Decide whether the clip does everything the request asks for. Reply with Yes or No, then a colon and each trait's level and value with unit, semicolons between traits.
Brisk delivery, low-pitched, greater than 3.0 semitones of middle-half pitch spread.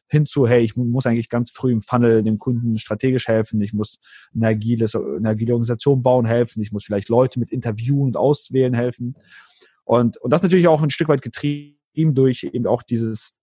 No: fast, 195 wpm; low, 120 Hz; average, 2.7 semitones